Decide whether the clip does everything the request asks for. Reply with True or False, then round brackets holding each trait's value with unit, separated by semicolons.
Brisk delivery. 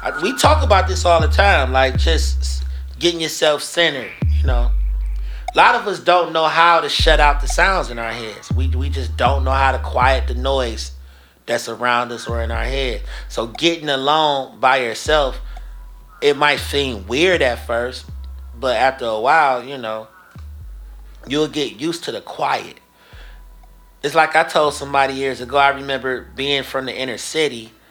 False (180 wpm)